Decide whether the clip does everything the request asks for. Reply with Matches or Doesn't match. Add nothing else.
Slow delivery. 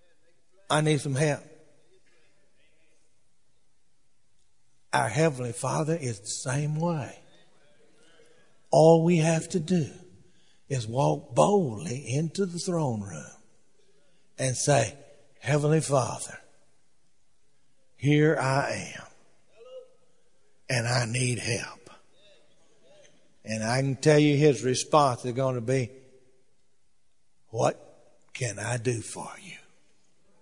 Matches